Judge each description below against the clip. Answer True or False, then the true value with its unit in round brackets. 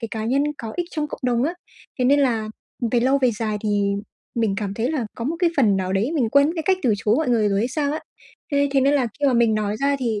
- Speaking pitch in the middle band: False (245 Hz)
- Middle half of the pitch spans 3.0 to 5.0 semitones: True (4.6 semitones)